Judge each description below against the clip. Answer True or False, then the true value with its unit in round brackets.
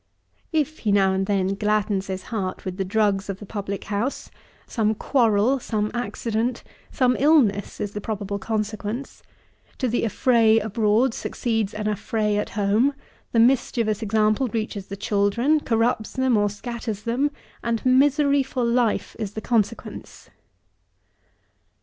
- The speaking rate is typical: True (145 wpm)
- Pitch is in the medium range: False (220 Hz)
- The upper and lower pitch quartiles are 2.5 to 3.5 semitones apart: True (3.0 semitones)